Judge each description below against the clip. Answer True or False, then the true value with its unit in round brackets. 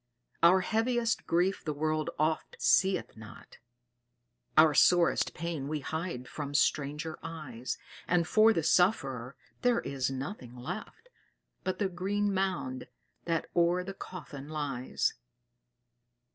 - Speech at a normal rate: False (120 wpm)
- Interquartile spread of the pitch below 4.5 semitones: False (4.8 semitones)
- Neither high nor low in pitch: True (165 Hz)